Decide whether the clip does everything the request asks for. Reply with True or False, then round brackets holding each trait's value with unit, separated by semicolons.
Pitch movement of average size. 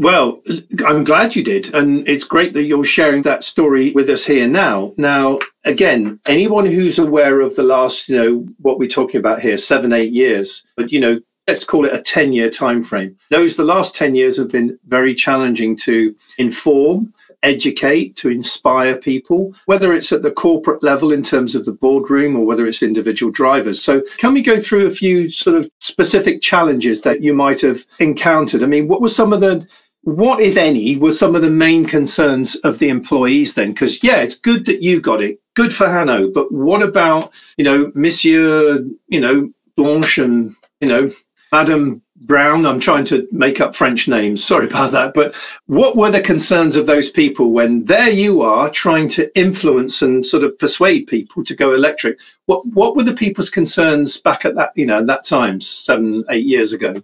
False (5.7 semitones)